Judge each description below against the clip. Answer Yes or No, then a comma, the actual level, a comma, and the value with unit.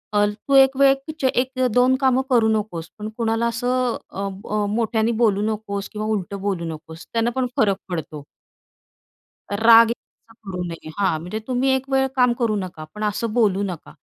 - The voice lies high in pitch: Yes, high, 220 Hz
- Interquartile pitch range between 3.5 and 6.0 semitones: Yes, average, 3.8 semitones